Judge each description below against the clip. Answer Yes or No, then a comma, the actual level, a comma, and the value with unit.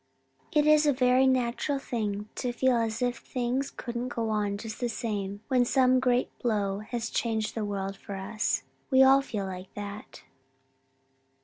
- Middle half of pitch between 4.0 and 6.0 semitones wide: No, average, 3.5 semitones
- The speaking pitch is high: Yes, high, 235 Hz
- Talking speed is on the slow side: No, average, 170 wpm